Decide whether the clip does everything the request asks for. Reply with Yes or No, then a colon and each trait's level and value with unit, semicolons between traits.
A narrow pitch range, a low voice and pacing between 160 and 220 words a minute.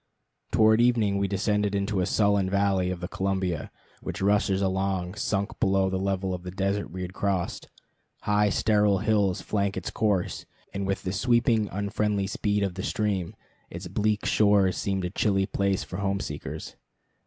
Yes: narrow, 1.5 semitones; low, 100 Hz; average, 170 wpm